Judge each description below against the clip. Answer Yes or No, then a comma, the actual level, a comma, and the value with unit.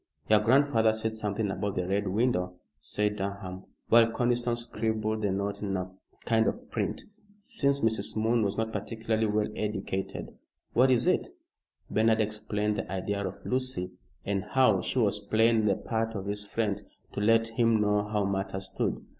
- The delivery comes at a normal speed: Yes, average, 170 wpm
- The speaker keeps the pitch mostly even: Yes, narrow, 2.1 semitones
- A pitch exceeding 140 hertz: No, low, 110 Hz